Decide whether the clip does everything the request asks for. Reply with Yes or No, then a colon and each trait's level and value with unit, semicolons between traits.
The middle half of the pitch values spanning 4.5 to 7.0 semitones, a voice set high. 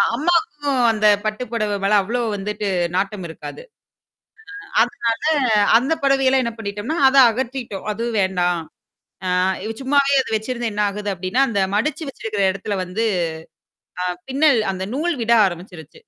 Yes: average, 4.8 semitones; high, 225 Hz